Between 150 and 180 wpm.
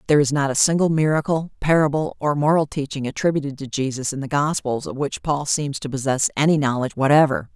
No: average, 200 wpm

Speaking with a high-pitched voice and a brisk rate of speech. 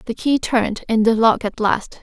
Yes: high, 225 Hz; fast, 235 wpm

